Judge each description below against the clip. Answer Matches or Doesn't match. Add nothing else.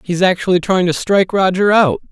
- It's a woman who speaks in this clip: Doesn't match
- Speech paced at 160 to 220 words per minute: Matches